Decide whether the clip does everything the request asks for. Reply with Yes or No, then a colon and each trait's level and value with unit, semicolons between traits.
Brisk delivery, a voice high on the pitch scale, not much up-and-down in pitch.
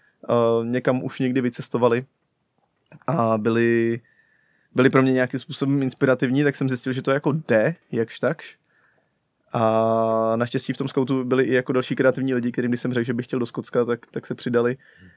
No: fast, 180 wpm; low, 130 Hz; narrow, 2.0 semitones